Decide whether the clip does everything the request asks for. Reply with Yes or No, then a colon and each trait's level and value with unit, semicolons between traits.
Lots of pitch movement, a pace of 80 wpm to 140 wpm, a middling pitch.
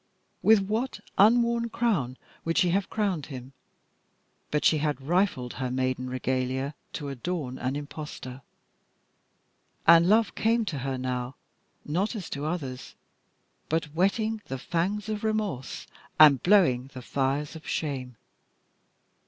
Yes: wide, 7.4 semitones; slow, 135 wpm; medium, 150 Hz